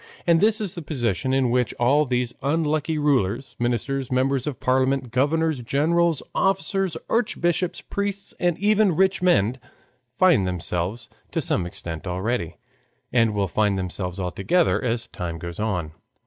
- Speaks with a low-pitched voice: Yes, low, 130 Hz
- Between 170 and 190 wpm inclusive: No, average, 145 wpm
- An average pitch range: No, wide, 8.0 semitones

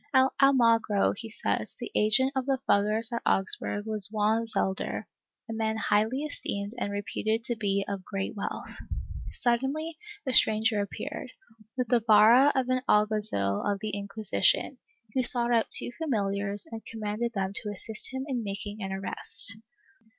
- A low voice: No, high, 220 Hz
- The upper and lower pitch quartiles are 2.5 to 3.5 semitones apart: Yes, average, 2.9 semitones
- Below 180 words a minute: Yes, average, 160 wpm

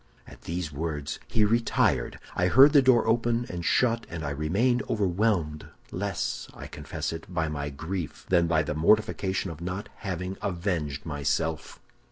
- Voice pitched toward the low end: Yes, very low, 90 Hz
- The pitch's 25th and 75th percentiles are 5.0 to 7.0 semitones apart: Yes, average, 5.3 semitones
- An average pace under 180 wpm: Yes, average, 160 wpm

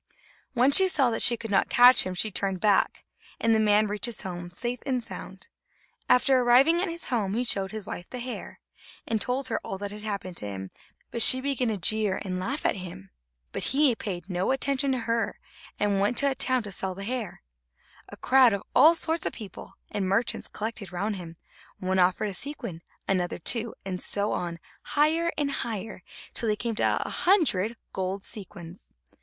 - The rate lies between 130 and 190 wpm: No, average, 200 wpm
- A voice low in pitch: No, high, 215 Hz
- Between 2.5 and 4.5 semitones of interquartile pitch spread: No, average, 4.9 semitones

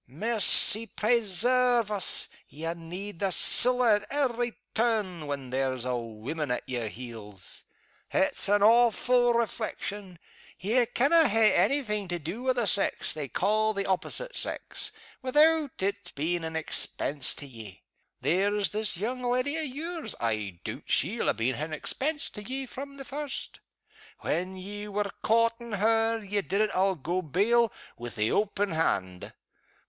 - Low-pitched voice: No, high, 205 Hz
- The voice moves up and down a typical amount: No, wide, 6.8 semitones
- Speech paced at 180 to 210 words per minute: No, average, 155 wpm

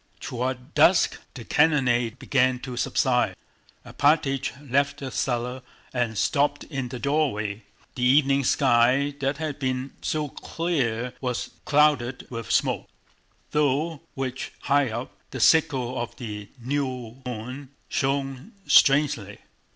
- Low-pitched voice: Yes, low, 130 Hz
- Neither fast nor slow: No, slow, 120 wpm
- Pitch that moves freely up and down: No, average, 2.7 semitones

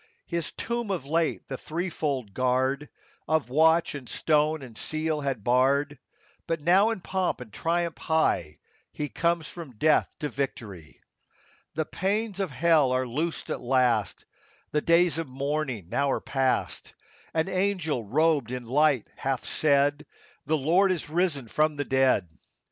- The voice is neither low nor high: Yes, medium, 150 Hz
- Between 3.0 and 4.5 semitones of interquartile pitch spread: Yes, average, 4.2 semitones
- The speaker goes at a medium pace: Yes, average, 155 wpm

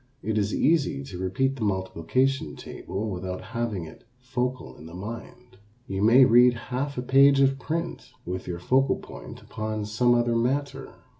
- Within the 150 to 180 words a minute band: Yes, average, 165 wpm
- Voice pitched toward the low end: Yes, low, 120 Hz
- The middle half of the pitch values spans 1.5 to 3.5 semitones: No, wide, 5.4 semitones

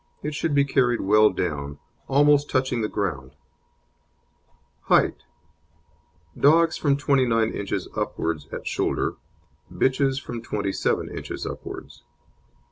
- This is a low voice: Yes, low, 120 Hz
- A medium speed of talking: No, slow, 110 wpm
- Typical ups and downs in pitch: No, wide, 5.9 semitones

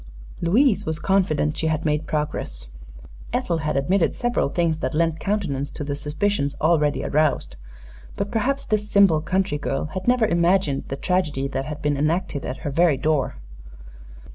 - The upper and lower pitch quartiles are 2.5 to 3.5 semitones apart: No, average, 4.5 semitones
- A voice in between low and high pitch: Yes, medium, 155 Hz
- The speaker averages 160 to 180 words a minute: Yes, average, 165 wpm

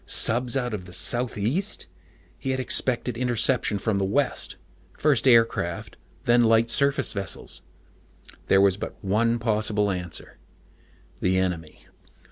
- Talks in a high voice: No, low, 115 Hz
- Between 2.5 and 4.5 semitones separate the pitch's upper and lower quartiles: Yes, average, 4.0 semitones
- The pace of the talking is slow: Yes, slow, 125 wpm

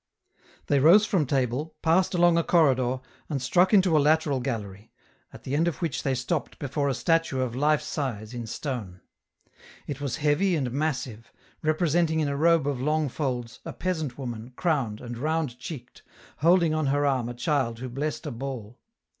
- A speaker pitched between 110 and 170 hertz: Yes, medium, 140 Hz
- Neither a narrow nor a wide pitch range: Yes, average, 4.2 semitones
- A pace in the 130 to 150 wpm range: No, average, 180 wpm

